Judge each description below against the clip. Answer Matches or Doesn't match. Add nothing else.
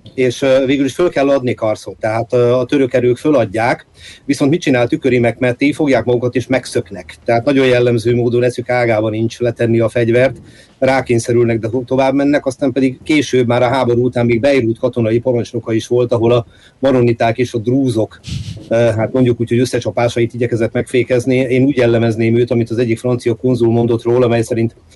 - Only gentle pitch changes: Matches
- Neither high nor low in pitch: Doesn't match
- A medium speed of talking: Doesn't match